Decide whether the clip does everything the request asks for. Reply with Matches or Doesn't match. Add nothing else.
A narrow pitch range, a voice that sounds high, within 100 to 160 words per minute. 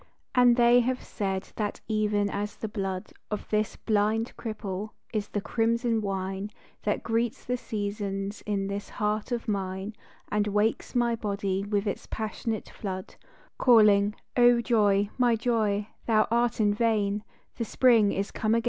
Matches